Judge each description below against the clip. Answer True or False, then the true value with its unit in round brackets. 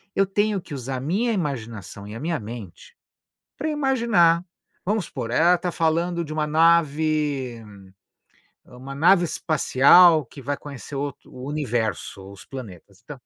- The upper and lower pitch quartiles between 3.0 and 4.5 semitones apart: False (5.5 semitones)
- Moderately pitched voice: True (150 Hz)